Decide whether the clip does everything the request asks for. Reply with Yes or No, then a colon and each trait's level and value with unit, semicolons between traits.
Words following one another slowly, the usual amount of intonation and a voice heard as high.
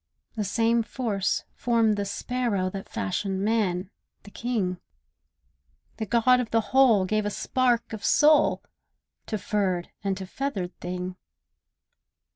Yes: slow, 130 wpm; average, 3.7 semitones; high, 210 Hz